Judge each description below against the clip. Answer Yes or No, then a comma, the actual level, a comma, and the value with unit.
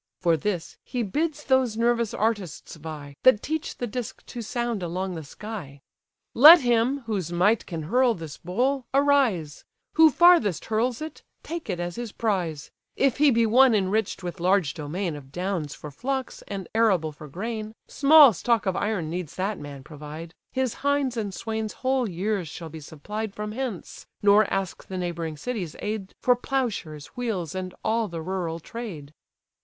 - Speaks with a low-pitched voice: No, high, 205 Hz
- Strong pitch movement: Yes, wide, 6.1 semitones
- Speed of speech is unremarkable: Yes, average, 170 wpm